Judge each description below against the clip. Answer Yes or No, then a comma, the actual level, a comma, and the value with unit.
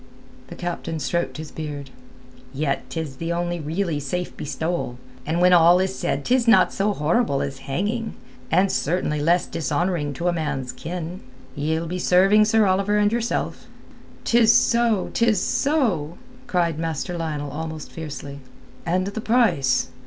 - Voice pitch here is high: No, medium, 170 Hz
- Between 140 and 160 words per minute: Yes, average, 150 wpm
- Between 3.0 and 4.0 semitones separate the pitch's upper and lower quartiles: No, average, 4.5 semitones